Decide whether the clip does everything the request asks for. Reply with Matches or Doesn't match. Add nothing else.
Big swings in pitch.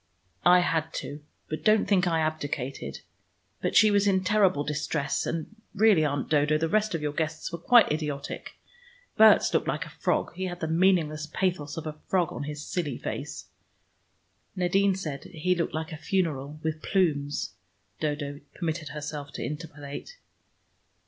Doesn't match